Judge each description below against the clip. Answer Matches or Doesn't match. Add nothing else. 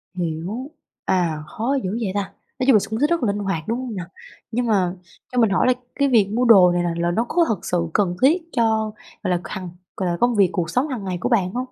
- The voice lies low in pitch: Doesn't match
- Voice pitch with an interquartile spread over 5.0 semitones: Matches